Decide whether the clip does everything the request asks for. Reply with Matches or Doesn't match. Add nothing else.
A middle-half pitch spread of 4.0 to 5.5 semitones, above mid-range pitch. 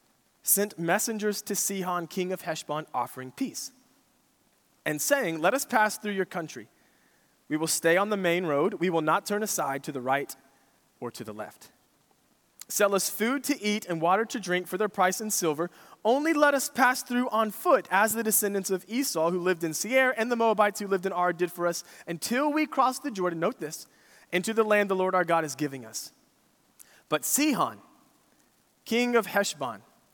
Matches